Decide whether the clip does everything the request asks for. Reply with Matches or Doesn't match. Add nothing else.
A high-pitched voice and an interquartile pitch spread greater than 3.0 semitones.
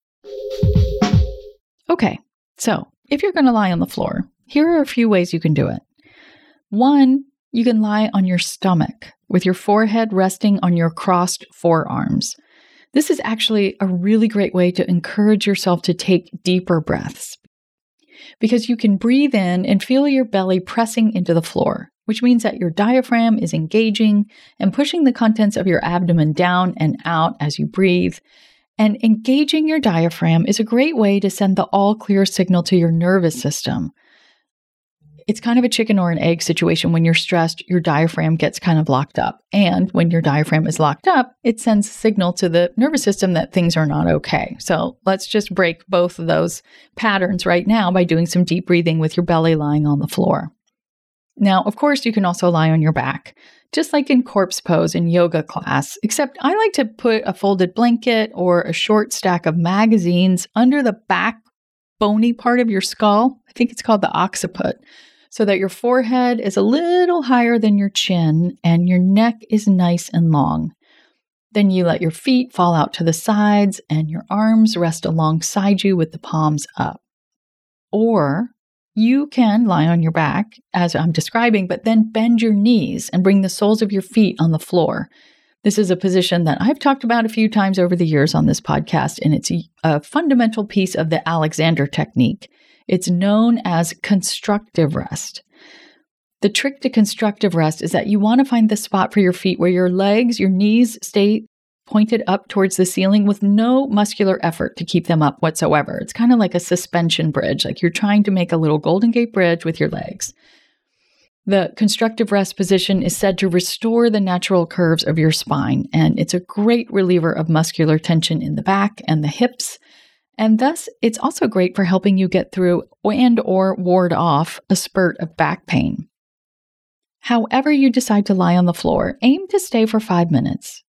Matches